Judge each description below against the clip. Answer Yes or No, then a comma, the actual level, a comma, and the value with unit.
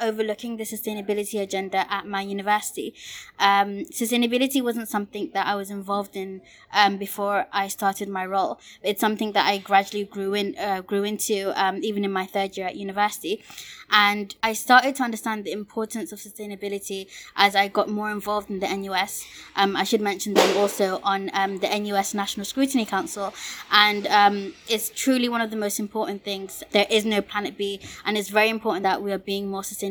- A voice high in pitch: Yes, high, 205 Hz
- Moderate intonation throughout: No, narrow, 1.4 semitones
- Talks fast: No, average, 190 wpm